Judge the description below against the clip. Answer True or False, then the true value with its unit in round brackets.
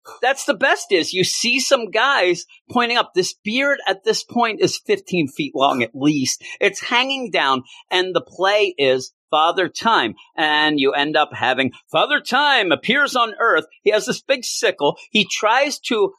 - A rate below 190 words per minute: True (180 wpm)